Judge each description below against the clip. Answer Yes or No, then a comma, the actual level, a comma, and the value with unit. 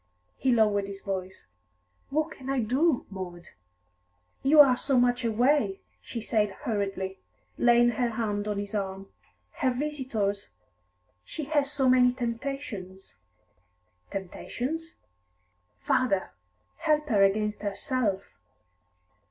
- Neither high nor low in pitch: No, high, 230 Hz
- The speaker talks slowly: Yes, slow, 115 wpm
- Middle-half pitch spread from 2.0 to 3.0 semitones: No, average, 5.1 semitones